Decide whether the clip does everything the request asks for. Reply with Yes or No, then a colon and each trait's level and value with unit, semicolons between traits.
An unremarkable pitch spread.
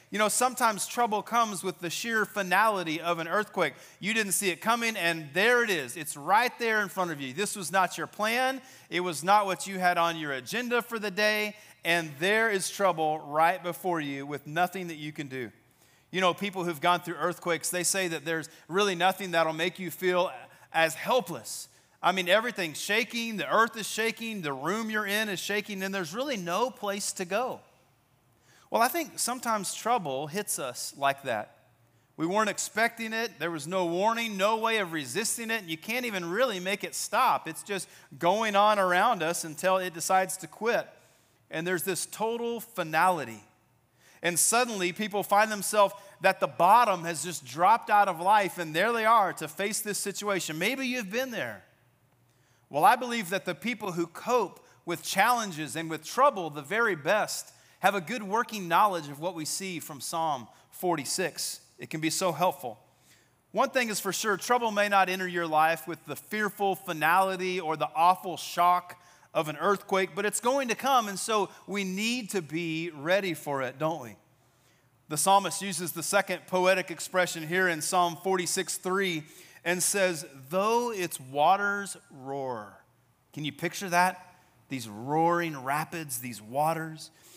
Yes: average, 4.1 semitones